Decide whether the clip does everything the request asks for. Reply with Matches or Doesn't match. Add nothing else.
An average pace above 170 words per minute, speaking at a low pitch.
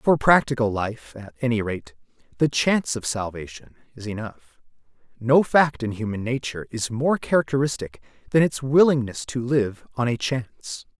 Doesn't match